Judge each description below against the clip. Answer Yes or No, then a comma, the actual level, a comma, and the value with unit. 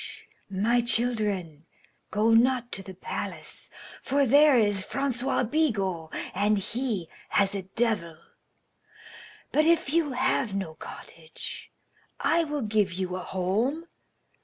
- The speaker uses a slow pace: Yes, slow, 120 wpm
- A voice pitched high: Yes, high, 220 Hz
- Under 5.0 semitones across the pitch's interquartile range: No, wide, 5.6 semitones